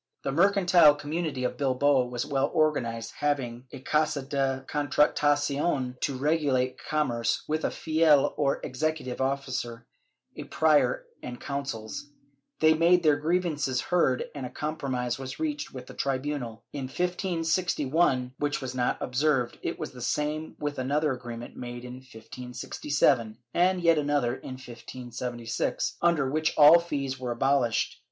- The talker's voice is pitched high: No, medium, 140 Hz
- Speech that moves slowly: No, average, 145 wpm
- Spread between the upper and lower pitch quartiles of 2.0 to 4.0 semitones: Yes, average, 3.4 semitones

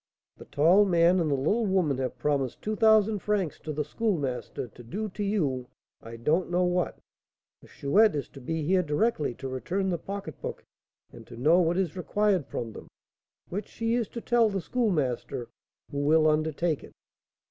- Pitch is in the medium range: Yes, medium, 170 Hz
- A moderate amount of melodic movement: No, wide, 6.1 semitones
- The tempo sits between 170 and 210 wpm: Yes, average, 180 wpm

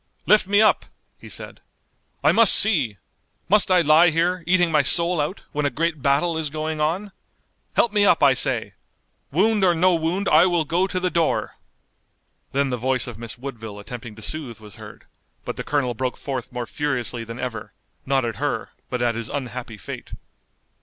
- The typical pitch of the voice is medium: Yes, medium, 150 Hz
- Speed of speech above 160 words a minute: Yes, average, 190 wpm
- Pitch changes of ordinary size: No, wide, 6.1 semitones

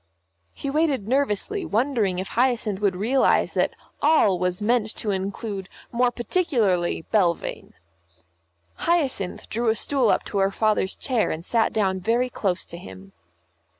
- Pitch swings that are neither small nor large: Yes, average, 4.9 semitones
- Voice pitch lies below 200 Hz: No, high, 215 Hz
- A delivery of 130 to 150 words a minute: Yes, average, 145 wpm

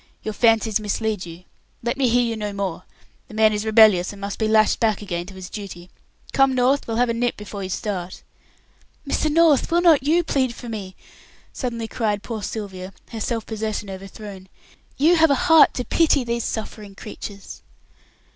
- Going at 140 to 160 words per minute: No, average, 185 wpm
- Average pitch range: Yes, average, 3.6 semitones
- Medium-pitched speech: No, high, 220 Hz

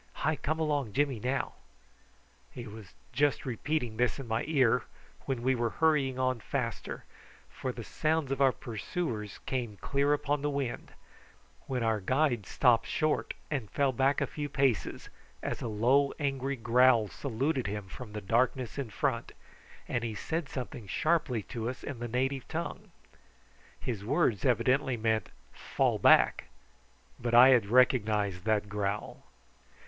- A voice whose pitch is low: Yes, low, 125 Hz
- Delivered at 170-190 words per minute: No, average, 155 wpm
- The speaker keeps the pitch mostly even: No, average, 3.8 semitones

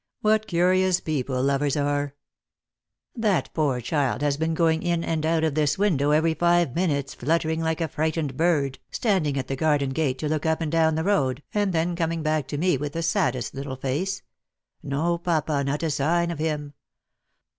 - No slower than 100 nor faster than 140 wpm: No, average, 200 wpm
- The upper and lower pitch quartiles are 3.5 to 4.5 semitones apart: No, average, 3.0 semitones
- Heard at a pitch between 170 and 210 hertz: No, medium, 155 Hz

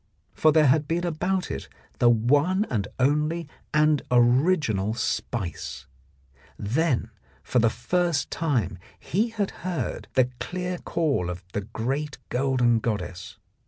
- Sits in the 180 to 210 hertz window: No, medium, 140 Hz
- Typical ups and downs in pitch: No, wide, 6.3 semitones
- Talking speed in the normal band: No, slow, 125 wpm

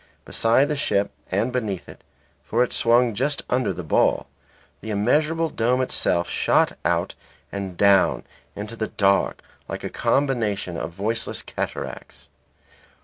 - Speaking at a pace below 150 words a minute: Yes, average, 140 wpm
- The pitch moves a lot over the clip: No, average, 4.2 semitones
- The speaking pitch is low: Yes, low, 110 Hz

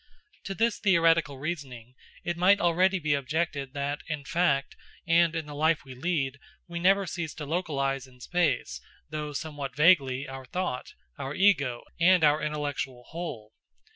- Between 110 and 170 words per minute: Yes, average, 155 wpm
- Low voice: No, medium, 150 Hz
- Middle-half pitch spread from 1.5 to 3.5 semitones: No, average, 3.9 semitones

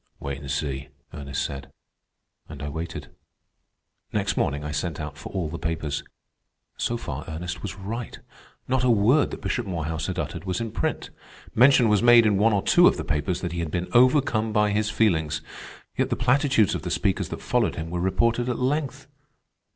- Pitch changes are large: Yes, wide, 7.1 semitones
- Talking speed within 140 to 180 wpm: No, average, 195 wpm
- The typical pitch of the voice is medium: No, very low, 95 Hz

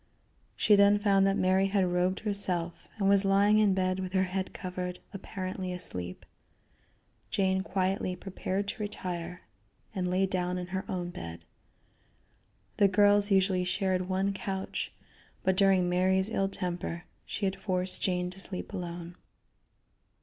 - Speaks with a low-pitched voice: No, high, 190 Hz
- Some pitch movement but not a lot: No, narrow, 1.4 semitones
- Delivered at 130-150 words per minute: Yes, average, 145 wpm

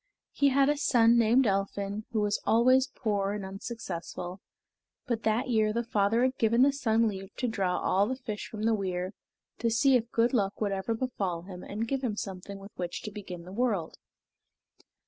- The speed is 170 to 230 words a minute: Yes, average, 195 wpm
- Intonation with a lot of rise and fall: No, average, 3.3 semitones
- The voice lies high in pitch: Yes, high, 215 Hz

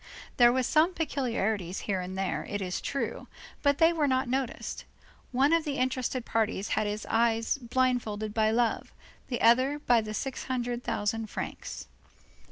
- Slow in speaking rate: No, average, 165 wpm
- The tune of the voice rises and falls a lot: No, average, 3.4 semitones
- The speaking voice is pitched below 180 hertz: No, high, 240 Hz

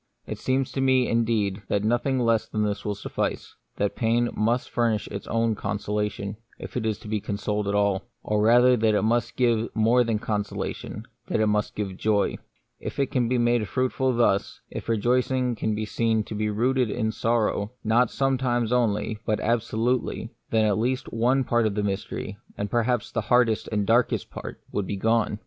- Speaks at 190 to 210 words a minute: Yes, average, 200 wpm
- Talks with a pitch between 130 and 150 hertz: No, low, 110 Hz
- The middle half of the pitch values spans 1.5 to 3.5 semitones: Yes, narrow, 2.4 semitones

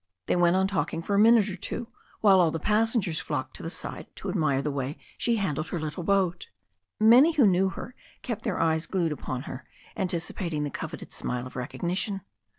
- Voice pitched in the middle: Yes, medium, 180 Hz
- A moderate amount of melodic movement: Yes, average, 4.7 semitones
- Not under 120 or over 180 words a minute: No, average, 200 wpm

